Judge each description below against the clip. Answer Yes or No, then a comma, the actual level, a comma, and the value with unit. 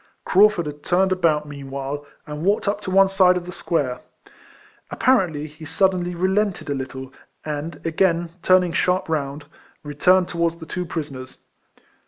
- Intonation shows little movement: No, average, 4.1 semitones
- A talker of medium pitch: Yes, medium, 170 Hz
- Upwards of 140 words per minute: Yes, average, 155 wpm